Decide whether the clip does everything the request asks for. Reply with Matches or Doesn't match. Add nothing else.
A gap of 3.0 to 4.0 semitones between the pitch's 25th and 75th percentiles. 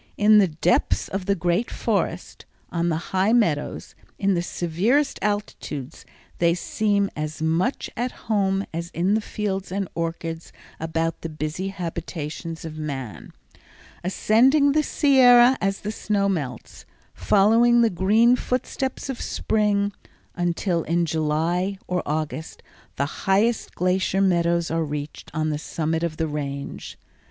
Doesn't match